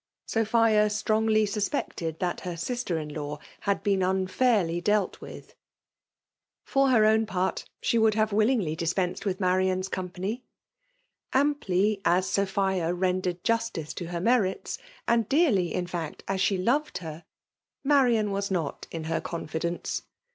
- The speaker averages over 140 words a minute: No, slow, 135 wpm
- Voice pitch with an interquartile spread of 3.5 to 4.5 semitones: Yes, average, 3.8 semitones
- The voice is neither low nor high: No, high, 195 Hz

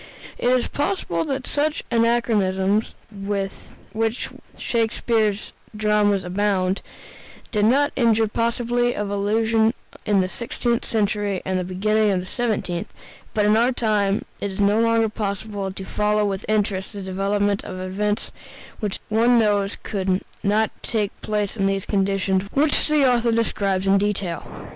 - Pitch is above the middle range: Yes, high, 210 Hz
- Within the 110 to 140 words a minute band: No, average, 150 wpm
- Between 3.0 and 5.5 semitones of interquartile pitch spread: No, narrow, 2.6 semitones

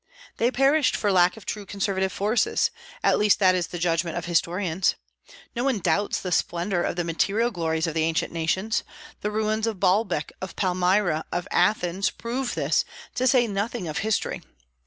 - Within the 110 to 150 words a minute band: No, average, 175 wpm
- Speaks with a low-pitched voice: No, high, 190 Hz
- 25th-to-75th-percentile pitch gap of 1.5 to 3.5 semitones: No, average, 4.0 semitones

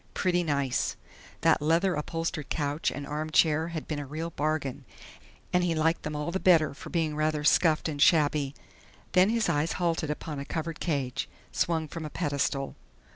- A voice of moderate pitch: Yes, medium, 155 Hz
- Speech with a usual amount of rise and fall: No, narrow, 2.2 semitones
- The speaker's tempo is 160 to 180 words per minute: Yes, average, 175 wpm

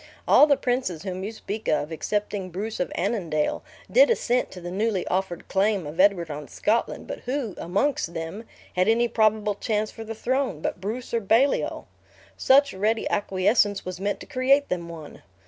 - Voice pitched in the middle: No, high, 205 Hz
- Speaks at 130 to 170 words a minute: No, average, 180 wpm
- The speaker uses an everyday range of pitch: Yes, average, 4.1 semitones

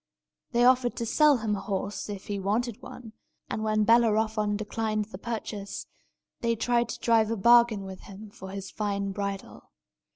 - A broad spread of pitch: No, narrow, 2.6 semitones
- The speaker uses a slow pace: No, average, 170 wpm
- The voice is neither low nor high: No, high, 215 Hz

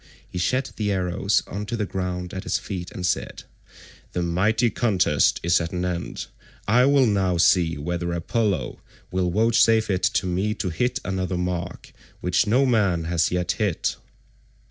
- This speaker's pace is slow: No, average, 165 wpm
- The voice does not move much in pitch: No, average, 3.3 semitones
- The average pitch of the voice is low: Yes, very low, 95 Hz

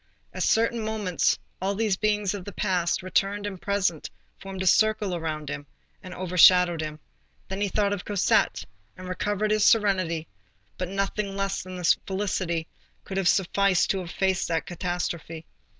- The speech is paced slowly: No, average, 160 wpm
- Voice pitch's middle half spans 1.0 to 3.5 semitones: Yes, narrow, 2.4 semitones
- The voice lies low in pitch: No, high, 190 Hz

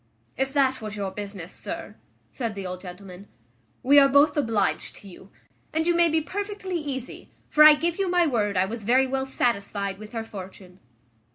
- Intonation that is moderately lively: No, wide, 7.0 semitones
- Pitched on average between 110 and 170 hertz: No, high, 240 Hz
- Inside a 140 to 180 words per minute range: No, average, 190 wpm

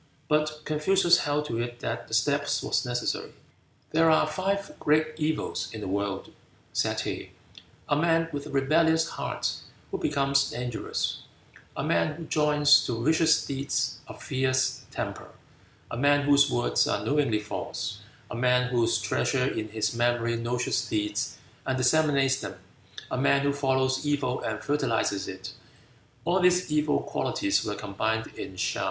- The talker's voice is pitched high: No, low, 135 Hz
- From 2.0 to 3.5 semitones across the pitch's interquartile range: No, average, 4.4 semitones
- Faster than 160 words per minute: No, average, 155 wpm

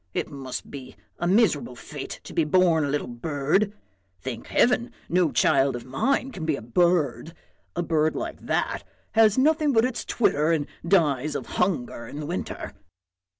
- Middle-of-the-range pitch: Yes, medium, 155 Hz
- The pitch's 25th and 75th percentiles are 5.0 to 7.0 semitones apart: Yes, wide, 5.6 semitones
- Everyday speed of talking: Yes, average, 170 wpm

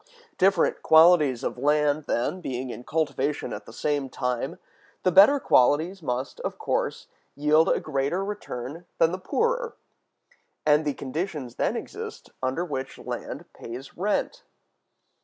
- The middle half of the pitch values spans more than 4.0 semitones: Yes, average, 5.2 semitones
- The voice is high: No, medium, 150 Hz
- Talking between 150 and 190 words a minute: No, average, 140 wpm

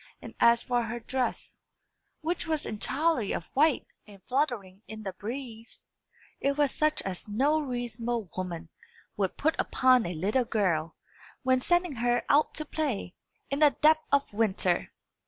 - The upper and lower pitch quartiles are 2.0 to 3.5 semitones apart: No, wide, 5.6 semitones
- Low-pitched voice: No, high, 240 Hz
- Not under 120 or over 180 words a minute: Yes, average, 155 wpm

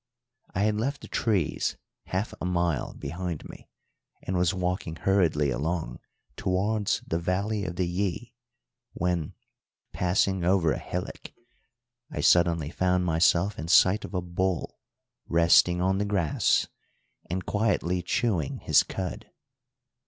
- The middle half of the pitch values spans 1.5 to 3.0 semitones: Yes, narrow, 2.4 semitones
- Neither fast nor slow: No, slow, 130 wpm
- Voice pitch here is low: Yes, very low, 90 Hz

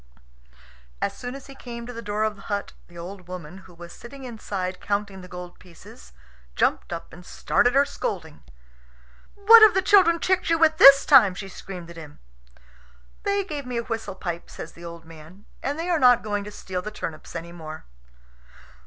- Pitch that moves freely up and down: Yes, wide, 7.5 semitones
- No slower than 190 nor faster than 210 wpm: Yes, average, 195 wpm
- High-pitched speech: Yes, high, 205 Hz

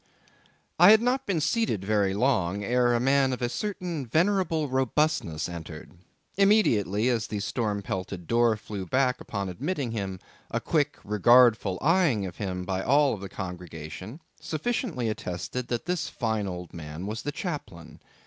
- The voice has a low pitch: Yes, low, 115 Hz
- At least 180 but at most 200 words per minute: No, average, 155 wpm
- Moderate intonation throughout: No, wide, 7.4 semitones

